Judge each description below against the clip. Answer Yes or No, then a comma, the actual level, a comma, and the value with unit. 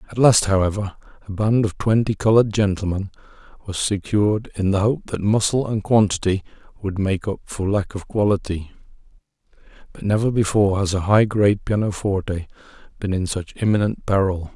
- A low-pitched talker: Yes, low, 100 Hz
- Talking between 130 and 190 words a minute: Yes, average, 155 wpm